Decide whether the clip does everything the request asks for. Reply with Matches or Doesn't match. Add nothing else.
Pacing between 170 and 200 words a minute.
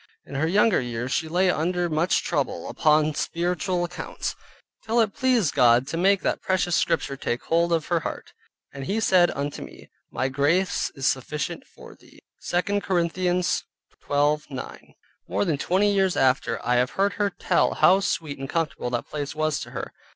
Matches